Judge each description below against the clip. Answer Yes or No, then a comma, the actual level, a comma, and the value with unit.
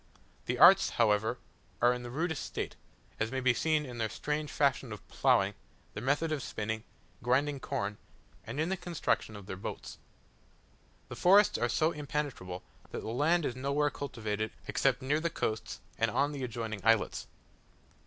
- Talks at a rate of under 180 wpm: Yes, average, 170 wpm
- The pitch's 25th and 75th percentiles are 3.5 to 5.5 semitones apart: Yes, average, 5.0 semitones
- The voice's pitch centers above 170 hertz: No, low, 130 Hz